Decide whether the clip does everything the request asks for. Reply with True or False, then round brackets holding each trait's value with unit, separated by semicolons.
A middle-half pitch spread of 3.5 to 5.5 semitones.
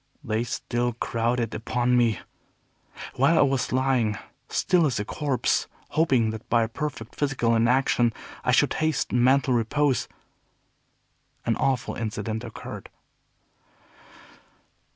False (2.9 semitones)